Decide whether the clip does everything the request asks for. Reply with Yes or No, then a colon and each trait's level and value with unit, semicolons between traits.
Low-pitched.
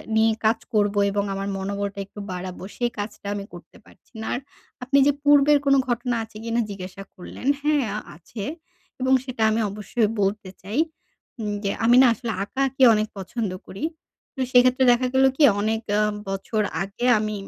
No: high, 220 Hz